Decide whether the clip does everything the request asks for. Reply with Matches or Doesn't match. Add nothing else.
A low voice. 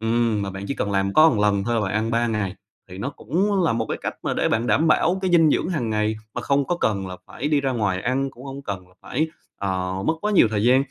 Matches